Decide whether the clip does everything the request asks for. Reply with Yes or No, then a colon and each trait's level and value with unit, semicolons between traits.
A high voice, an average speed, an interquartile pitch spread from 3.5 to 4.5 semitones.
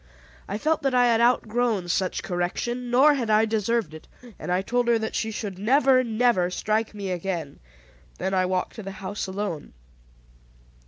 Yes: high, 215 Hz; average, 175 wpm; average, 4.2 semitones